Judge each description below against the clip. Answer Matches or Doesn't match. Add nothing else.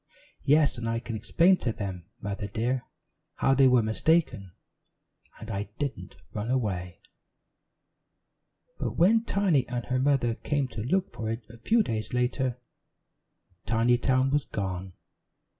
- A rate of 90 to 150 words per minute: Matches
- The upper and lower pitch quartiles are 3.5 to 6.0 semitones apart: Matches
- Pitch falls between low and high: Doesn't match